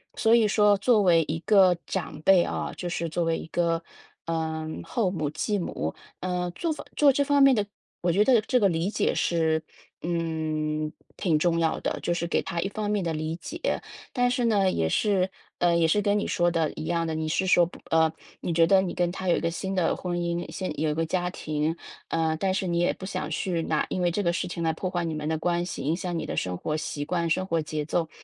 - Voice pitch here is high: No, medium, 175 Hz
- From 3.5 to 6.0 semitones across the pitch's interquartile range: No, average, 2.9 semitones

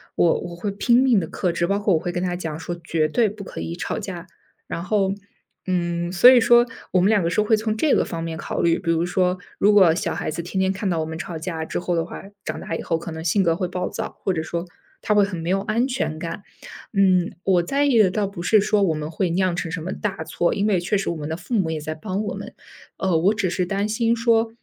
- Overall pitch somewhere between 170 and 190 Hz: Yes, medium, 185 Hz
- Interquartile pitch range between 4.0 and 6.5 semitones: No, average, 3.5 semitones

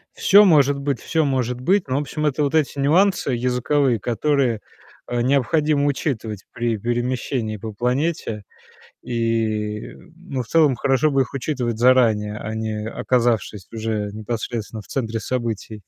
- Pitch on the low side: Yes, low, 125 Hz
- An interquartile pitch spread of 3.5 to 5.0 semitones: Yes, average, 4.1 semitones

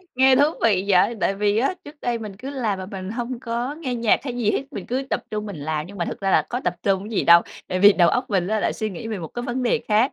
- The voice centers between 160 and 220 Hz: Yes, high, 215 Hz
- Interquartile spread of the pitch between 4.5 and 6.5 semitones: No, average, 4.1 semitones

